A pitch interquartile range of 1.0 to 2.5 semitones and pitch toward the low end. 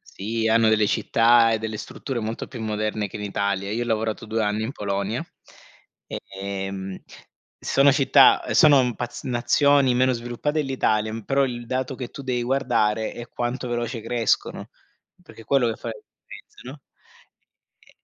No: average, 2.9 semitones; low, 115 Hz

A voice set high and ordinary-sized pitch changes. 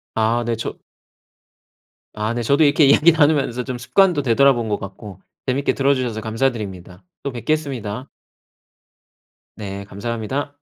No: low, 120 Hz; average, 4.4 semitones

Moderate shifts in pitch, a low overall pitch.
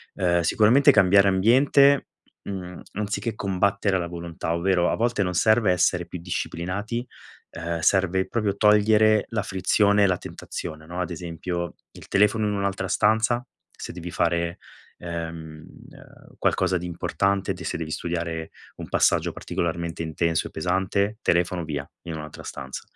Yes: average, 3.3 semitones; very low, 90 Hz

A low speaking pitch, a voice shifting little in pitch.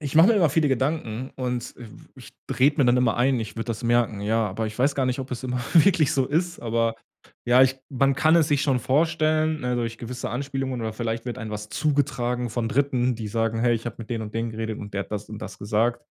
No: low, 125 Hz; average, 3.4 semitones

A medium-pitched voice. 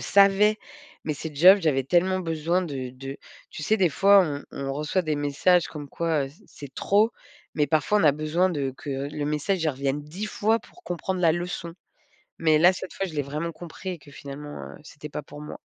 Yes: medium, 155 Hz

